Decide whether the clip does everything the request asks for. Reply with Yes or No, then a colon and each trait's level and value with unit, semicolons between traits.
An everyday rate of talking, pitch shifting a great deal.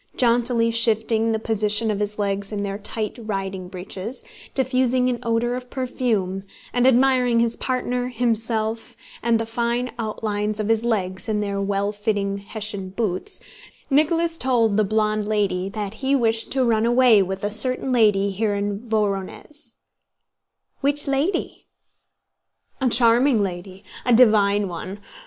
No: average, 145 wpm; average, 3.2 semitones